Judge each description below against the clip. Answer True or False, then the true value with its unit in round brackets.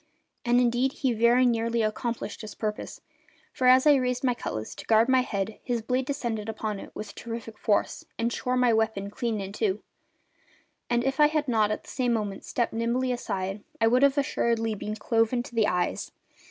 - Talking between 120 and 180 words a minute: False (195 wpm)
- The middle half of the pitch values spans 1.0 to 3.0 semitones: True (2.6 semitones)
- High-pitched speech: True (230 Hz)